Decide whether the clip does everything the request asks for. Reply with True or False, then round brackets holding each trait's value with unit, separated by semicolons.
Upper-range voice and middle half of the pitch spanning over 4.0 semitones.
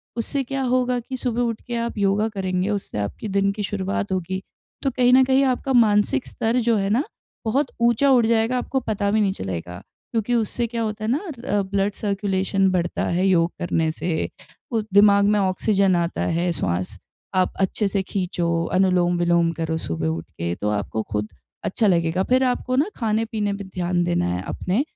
True (200 Hz; 4.9 semitones)